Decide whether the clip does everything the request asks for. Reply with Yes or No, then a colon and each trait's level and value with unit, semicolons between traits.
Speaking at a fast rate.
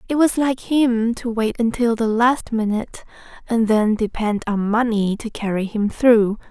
No: average, 175 wpm